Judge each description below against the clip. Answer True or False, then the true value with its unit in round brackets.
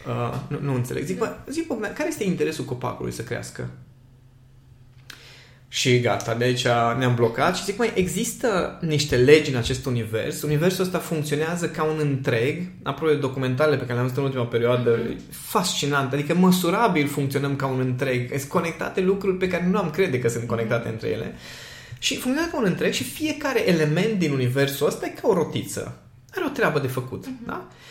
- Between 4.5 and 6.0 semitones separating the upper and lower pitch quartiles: True (5.6 semitones)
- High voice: False (140 Hz)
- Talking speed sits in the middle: False (185 wpm)